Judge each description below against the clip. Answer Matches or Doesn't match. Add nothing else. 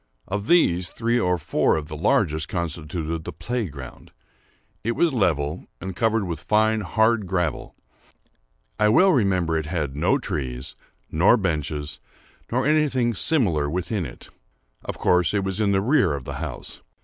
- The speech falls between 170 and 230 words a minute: Doesn't match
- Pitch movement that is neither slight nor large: Doesn't match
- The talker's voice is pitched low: Matches